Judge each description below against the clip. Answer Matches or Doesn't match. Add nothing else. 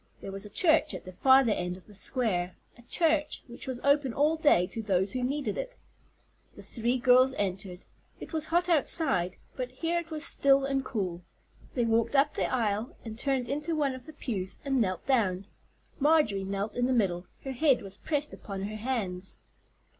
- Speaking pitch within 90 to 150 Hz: Doesn't match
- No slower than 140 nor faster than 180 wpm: Doesn't match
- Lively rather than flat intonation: Matches